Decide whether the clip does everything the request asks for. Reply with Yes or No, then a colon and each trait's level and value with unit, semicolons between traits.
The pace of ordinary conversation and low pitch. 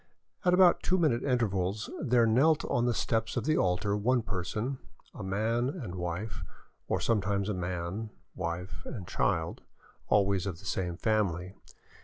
Yes: average, 155 wpm; low, 105 Hz